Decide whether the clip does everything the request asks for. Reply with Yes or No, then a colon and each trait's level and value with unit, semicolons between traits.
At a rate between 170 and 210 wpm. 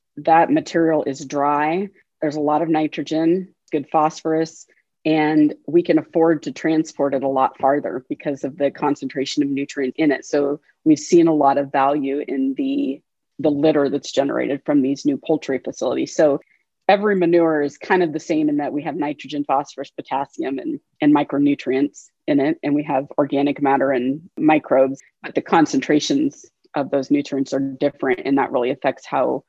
Yes: average, 175 wpm